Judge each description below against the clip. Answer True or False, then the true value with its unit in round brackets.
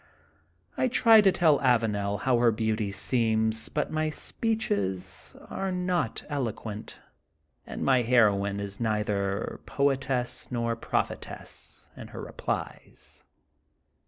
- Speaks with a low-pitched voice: True (115 Hz)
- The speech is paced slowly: True (110 wpm)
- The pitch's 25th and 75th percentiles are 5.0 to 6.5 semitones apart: True (5.4 semitones)